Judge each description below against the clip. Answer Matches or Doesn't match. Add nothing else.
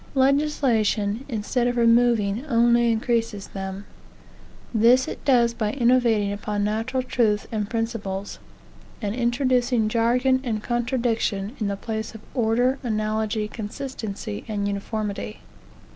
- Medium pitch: Doesn't match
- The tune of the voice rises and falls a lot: Doesn't match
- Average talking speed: Doesn't match